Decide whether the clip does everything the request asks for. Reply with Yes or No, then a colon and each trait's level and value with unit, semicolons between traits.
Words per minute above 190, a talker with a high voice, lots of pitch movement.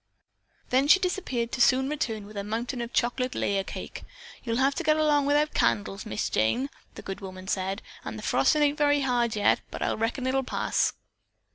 Yes: fast, 205 wpm; high, 245 Hz; wide, 5.7 semitones